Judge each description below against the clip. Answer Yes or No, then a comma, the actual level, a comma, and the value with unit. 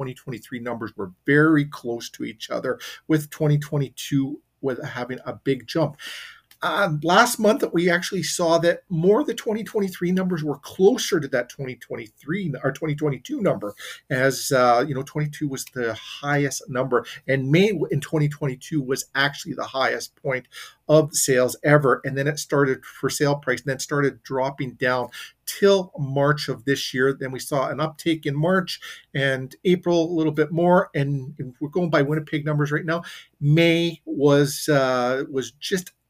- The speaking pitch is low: No, medium, 145 Hz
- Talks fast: No, average, 165 wpm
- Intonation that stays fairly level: No, average, 3.4 semitones